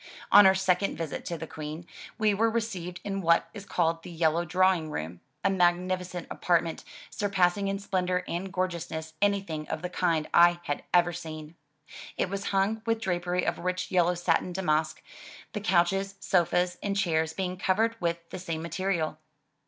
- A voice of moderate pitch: Yes, medium, 180 Hz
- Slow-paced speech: No, average, 170 wpm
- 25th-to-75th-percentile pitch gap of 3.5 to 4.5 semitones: No, narrow, 2.5 semitones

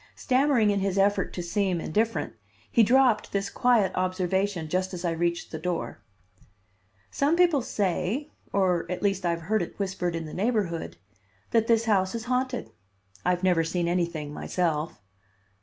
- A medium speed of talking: Yes, average, 160 wpm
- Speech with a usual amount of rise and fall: Yes, average, 4.4 semitones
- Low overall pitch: No, high, 190 Hz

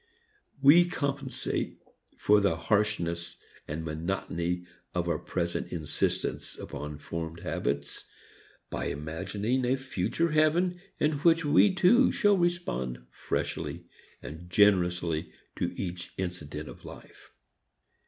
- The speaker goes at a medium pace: No, slow, 110 wpm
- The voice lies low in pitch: Yes, very low, 90 Hz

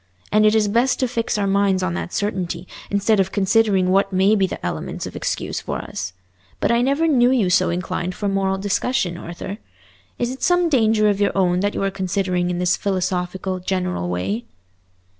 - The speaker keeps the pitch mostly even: No, average, 3.0 semitones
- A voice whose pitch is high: Yes, high, 195 Hz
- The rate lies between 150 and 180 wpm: No, average, 195 wpm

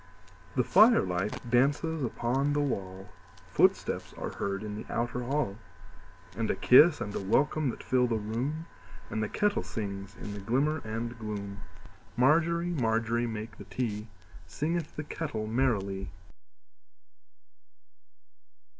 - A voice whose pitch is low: Yes, low, 115 Hz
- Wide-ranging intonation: Yes, wide, 5.8 semitones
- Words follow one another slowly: Yes, slow, 115 wpm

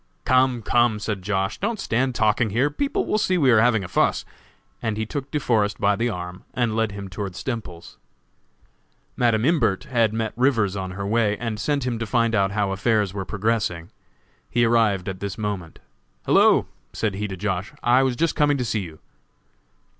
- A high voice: No, low, 110 Hz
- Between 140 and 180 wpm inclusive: No, average, 190 wpm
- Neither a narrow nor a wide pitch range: Yes, average, 3.4 semitones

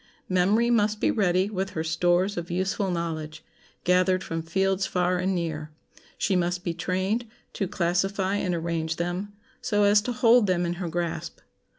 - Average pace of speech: Yes, average, 170 wpm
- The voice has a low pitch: No, medium, 180 Hz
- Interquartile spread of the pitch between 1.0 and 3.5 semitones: Yes, narrow, 2.4 semitones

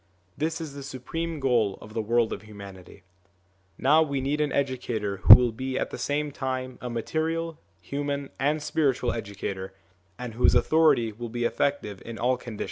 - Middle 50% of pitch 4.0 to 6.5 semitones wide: Yes, average, 4.3 semitones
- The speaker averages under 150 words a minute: No, average, 175 wpm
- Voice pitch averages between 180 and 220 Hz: No, low, 130 Hz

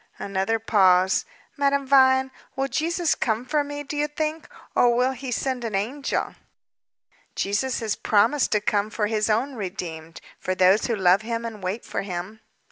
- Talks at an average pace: Yes, average, 170 wpm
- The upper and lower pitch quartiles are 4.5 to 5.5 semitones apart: Yes, average, 5.1 semitones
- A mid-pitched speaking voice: No, high, 225 Hz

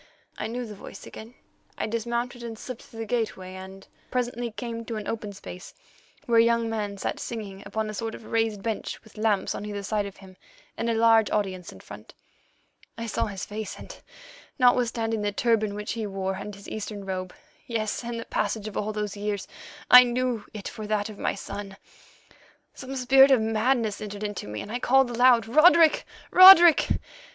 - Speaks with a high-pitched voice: Yes, high, 220 Hz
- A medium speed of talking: Yes, average, 190 wpm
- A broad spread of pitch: No, narrow, 2.6 semitones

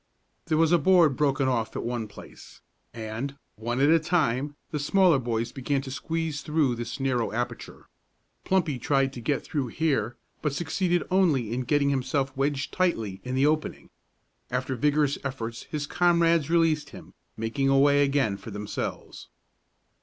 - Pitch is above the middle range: No, medium, 140 Hz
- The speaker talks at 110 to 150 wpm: No, average, 160 wpm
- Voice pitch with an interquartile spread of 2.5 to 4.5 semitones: Yes, average, 4.2 semitones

